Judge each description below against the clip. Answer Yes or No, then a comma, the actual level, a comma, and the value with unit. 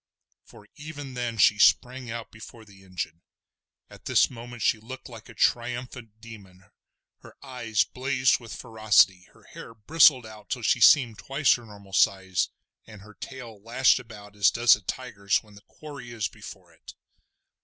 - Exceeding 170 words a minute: No, average, 165 wpm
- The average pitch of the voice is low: Yes, low, 115 Hz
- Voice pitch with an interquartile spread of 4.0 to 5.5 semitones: No, average, 3.4 semitones